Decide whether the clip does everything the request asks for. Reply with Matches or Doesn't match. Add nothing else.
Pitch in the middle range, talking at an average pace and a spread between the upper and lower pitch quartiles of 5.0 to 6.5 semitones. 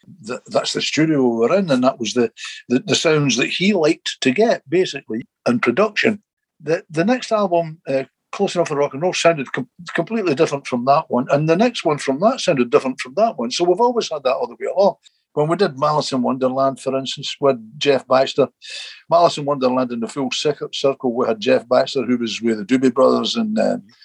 Doesn't match